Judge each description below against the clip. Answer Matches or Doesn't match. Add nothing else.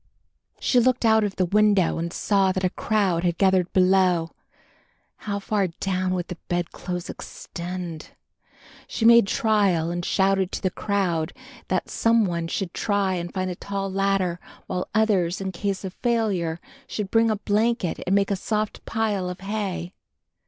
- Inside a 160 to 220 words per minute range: Matches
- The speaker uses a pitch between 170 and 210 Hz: Matches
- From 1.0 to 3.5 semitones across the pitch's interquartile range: Matches